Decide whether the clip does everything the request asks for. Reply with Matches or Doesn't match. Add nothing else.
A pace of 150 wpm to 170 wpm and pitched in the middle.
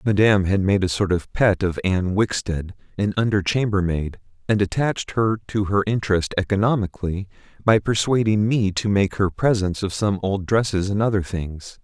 Doesn't match